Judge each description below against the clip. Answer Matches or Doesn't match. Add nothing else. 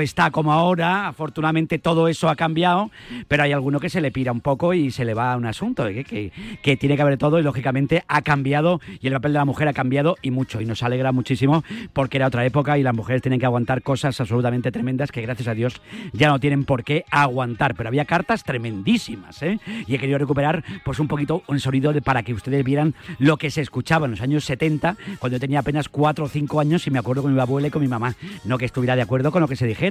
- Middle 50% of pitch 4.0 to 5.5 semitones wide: Doesn't match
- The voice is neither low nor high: Matches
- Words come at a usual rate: Doesn't match